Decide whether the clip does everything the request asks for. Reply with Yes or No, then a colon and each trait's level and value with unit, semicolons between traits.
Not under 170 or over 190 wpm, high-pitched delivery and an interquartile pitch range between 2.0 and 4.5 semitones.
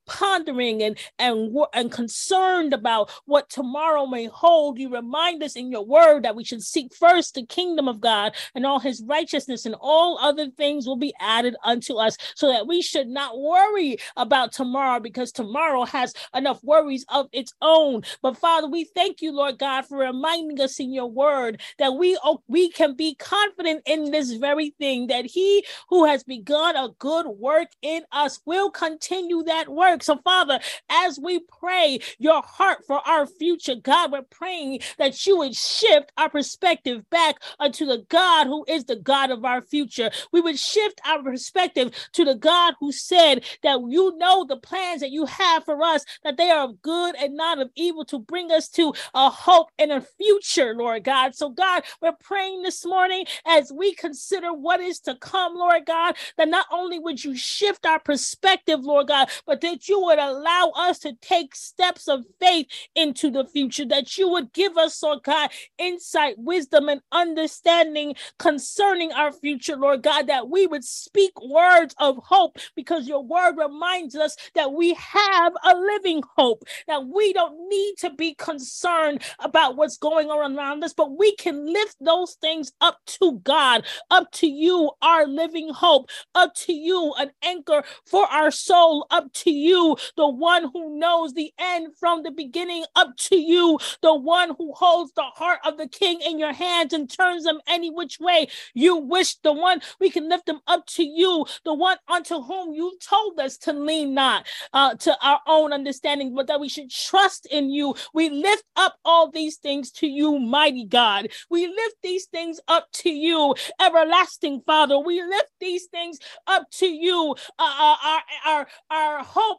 Yes: average, 185 wpm; very high, 315 Hz; average, 3.7 semitones